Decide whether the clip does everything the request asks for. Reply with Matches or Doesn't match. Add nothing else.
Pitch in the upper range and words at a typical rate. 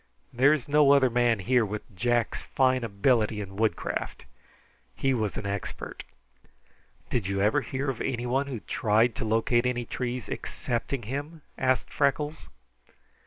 Doesn't match